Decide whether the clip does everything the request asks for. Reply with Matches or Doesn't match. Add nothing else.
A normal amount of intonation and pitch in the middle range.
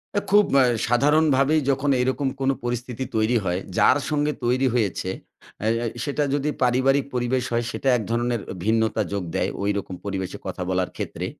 Doesn't match